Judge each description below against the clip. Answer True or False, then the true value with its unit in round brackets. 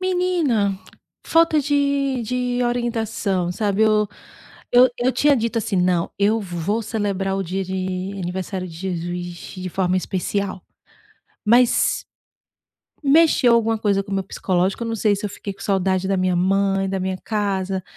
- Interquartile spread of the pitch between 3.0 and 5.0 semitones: True (4.0 semitones)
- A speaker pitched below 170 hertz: False (200 Hz)